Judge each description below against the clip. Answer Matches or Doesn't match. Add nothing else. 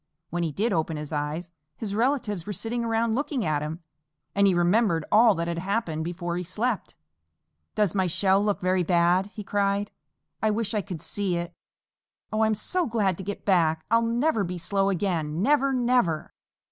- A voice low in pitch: Doesn't match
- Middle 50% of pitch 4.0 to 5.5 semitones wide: Matches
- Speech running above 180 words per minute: Matches